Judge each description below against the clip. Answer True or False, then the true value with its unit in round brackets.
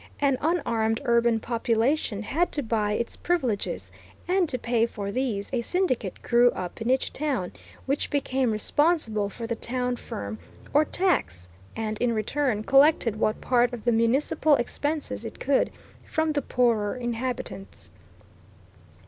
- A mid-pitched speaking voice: False (240 Hz)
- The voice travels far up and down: False (4.2 semitones)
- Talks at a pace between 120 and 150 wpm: True (145 wpm)